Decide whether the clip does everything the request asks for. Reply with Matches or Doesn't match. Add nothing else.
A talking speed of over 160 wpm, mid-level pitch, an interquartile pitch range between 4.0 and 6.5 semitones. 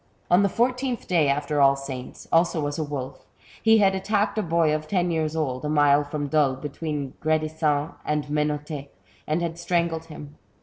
Doesn't match